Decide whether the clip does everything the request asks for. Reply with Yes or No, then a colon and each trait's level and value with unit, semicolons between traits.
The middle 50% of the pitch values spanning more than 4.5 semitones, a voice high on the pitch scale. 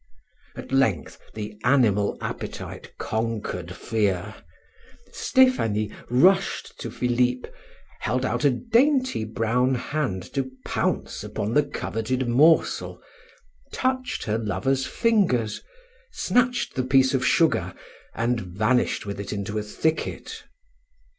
No: average, 5.1 semitones; low, 125 Hz